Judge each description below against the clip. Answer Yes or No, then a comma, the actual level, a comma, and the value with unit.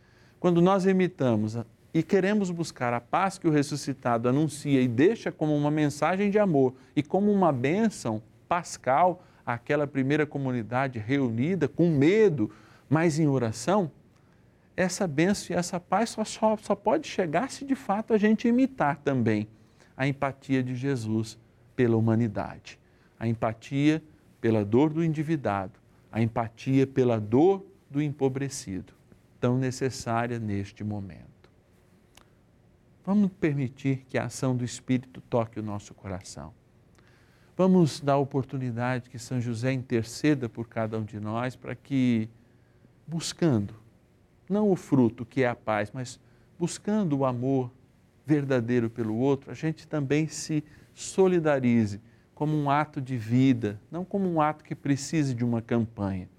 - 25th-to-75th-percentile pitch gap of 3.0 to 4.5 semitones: No, average, 5.3 semitones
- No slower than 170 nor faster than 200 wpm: No, average, 140 wpm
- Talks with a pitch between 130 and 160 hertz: Yes, low, 135 Hz